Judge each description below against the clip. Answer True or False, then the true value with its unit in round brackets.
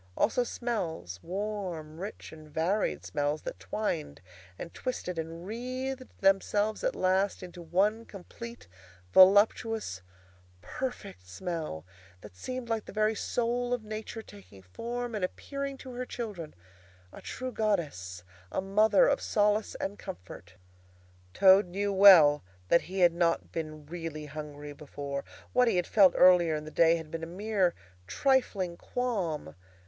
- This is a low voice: False (190 Hz)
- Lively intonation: True (5.9 semitones)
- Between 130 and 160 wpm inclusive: True (140 wpm)